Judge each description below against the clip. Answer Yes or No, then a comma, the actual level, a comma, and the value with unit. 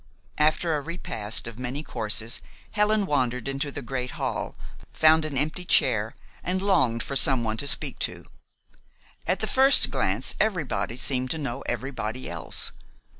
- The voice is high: No, low, 135 Hz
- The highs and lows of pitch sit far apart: No, average, 5.0 semitones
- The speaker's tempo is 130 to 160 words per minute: Yes, average, 150 wpm